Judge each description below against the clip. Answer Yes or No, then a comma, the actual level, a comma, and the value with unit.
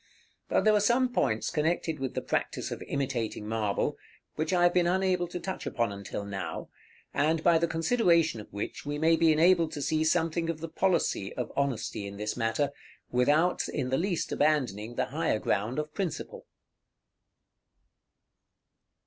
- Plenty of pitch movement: Yes, wide, 6.2 semitones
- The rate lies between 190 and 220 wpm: No, average, 165 wpm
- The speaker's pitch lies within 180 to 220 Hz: No, medium, 155 Hz